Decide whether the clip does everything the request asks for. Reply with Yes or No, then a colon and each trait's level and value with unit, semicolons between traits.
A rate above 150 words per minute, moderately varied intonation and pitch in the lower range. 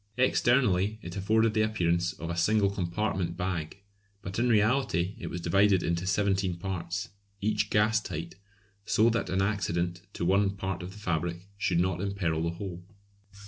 Yes: average, 165 wpm; average, 3.3 semitones; very low, 95 Hz